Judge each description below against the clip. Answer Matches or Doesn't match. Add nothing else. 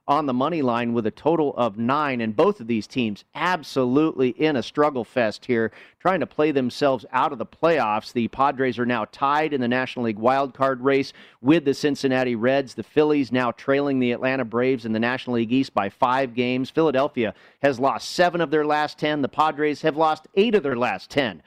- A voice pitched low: Matches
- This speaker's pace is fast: Matches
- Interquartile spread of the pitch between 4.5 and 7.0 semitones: Doesn't match